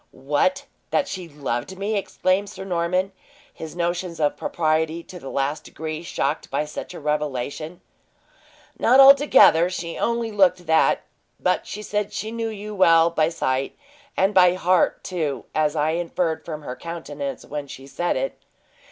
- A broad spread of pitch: No, average, 3.8 semitones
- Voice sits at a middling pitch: Yes, medium, 170 Hz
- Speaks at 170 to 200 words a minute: No, average, 160 wpm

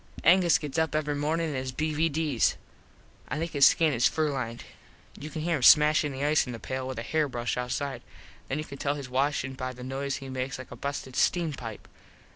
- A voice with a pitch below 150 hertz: Yes, medium, 140 Hz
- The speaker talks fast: Yes, fast, 220 wpm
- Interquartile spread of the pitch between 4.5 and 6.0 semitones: No, average, 3.0 semitones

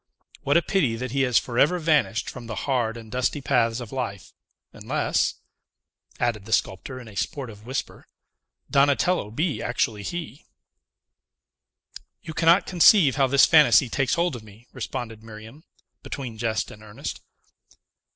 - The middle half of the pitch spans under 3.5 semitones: No, average, 4.2 semitones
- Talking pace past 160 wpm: No, average, 145 wpm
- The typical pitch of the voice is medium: No, low, 125 Hz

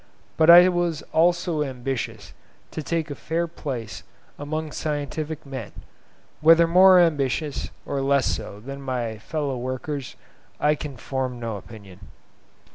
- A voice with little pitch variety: No, average, 3.9 semitones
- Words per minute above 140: No, slow, 135 wpm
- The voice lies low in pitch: No, medium, 145 Hz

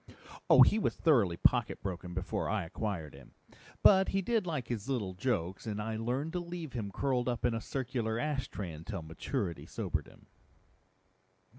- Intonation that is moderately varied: No, wide, 6.5 semitones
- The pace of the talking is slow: No, average, 170 wpm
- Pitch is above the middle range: No, low, 115 Hz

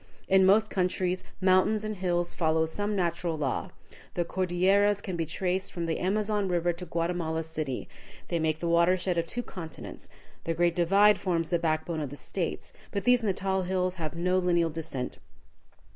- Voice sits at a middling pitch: Yes, medium, 175 Hz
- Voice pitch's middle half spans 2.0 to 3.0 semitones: Yes, narrow, 2.4 semitones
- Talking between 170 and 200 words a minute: Yes, average, 175 wpm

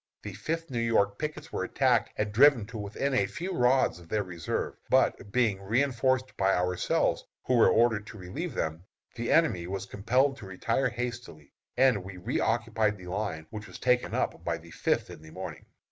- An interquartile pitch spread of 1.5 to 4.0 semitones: No, average, 4.8 semitones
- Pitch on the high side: No, low, 110 Hz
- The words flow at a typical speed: Yes, average, 190 wpm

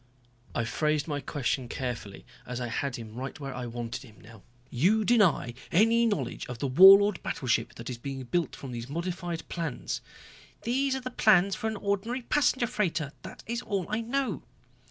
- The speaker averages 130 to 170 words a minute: No, average, 180 wpm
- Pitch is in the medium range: Yes, medium, 165 Hz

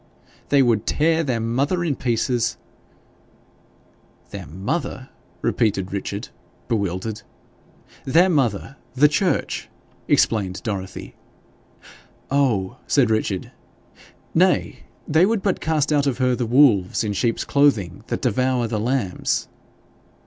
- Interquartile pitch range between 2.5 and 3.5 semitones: No, wide, 5.5 semitones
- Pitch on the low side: Yes, low, 125 Hz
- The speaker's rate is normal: No, slow, 115 wpm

